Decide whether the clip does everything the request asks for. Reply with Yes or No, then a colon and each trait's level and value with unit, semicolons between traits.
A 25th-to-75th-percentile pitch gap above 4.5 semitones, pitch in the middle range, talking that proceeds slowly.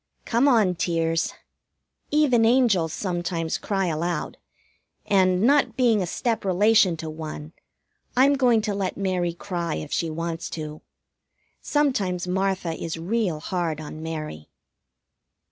Yes: average, 5.2 semitones; medium, 180 Hz; slow, 130 wpm